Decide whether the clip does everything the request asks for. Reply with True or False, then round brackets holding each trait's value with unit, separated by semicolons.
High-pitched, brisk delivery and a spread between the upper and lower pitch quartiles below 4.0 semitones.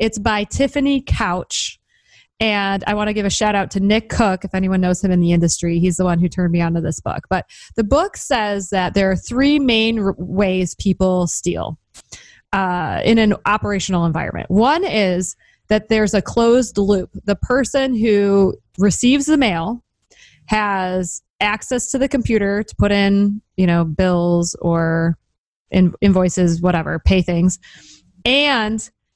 False (200 Hz; 165 wpm; 3.5 semitones)